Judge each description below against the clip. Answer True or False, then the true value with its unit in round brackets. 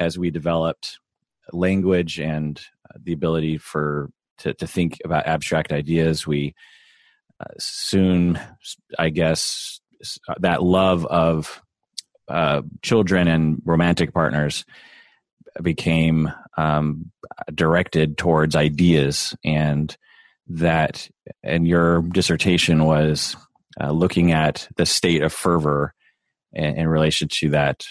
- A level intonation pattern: True (1.9 semitones)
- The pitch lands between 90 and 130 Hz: False (80 Hz)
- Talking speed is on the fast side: False (110 wpm)